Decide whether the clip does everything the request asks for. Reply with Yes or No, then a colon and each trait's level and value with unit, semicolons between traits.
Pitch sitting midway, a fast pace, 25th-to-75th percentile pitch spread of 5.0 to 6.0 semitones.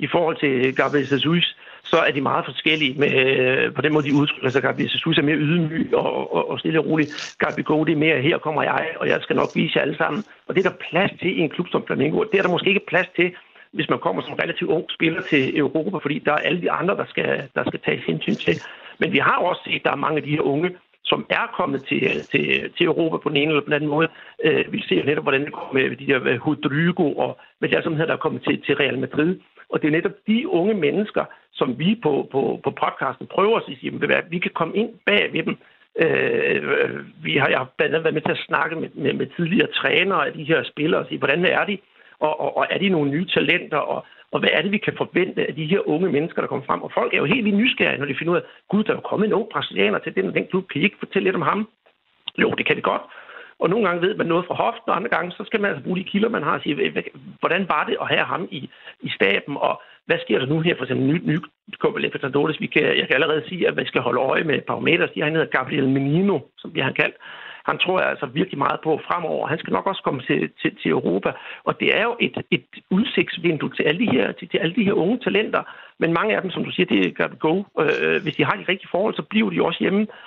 Yes: medium, 170 Hz; fast, 275 wpm; wide, 5.5 semitones